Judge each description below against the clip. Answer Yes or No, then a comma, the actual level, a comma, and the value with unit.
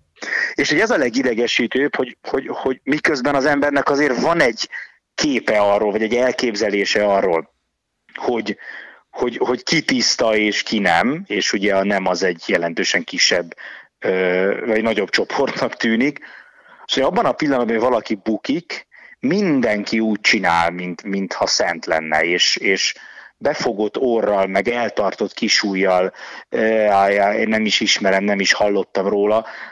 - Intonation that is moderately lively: No, narrow, 2.3 semitones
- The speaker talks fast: No, average, 140 wpm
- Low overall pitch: Yes, low, 100 Hz